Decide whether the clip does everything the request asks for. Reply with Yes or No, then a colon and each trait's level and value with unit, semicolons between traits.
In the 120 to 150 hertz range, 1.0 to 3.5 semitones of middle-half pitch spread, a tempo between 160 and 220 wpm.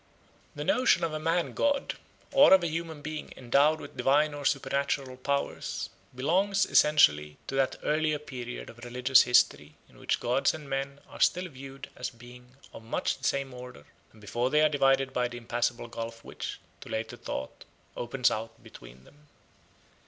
No: low, 135 Hz; average, 4.0 semitones; average, 175 wpm